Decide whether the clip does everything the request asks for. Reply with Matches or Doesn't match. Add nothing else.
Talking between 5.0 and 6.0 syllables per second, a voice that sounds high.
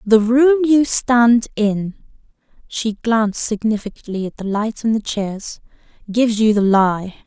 Doesn't match